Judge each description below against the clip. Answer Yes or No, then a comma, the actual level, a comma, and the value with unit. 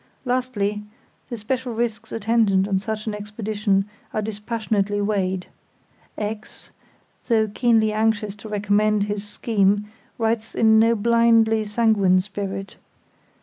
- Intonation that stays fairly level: Yes, narrow, 1.7 semitones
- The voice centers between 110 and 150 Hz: No, high, 215 Hz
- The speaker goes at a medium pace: No, slow, 115 wpm